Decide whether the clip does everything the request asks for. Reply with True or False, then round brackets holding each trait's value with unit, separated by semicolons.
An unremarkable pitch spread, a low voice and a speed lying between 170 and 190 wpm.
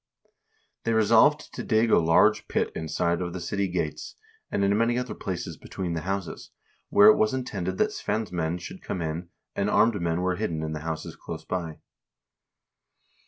True (4.3 semitones; 95 Hz; 180 wpm)